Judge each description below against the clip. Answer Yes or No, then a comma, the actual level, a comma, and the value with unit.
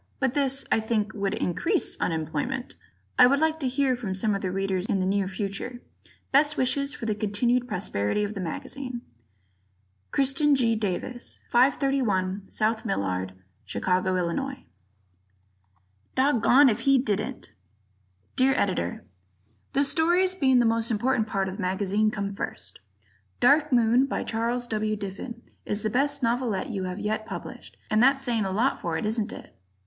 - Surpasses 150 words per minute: Yes, average, 160 wpm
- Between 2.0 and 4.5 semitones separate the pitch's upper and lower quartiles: No, average, 5.1 semitones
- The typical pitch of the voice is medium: No, high, 225 Hz